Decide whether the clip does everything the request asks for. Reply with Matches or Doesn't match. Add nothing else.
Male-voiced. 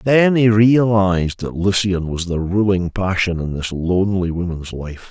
Matches